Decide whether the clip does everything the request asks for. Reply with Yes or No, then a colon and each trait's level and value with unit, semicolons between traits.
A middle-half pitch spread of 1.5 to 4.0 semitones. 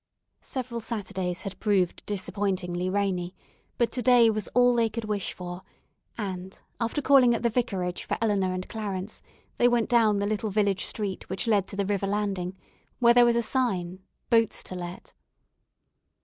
Yes: average, 3.7 semitones